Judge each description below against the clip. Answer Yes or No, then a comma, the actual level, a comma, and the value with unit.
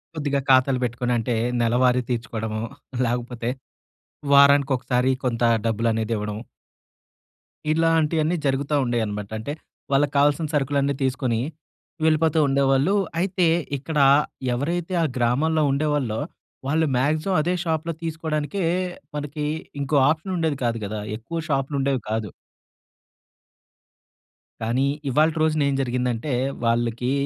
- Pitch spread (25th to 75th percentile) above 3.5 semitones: Yes, average, 4.3 semitones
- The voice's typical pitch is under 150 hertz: Yes, low, 135 Hz